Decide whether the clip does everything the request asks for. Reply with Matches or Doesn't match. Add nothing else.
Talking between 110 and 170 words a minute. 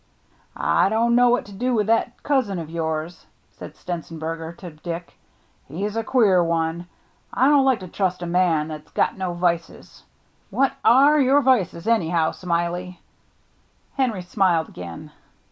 Matches